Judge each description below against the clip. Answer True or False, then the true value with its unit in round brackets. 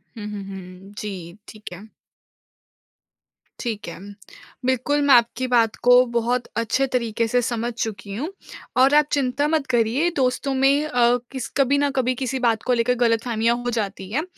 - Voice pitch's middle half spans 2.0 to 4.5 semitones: True (2.7 semitones)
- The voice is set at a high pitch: True (240 Hz)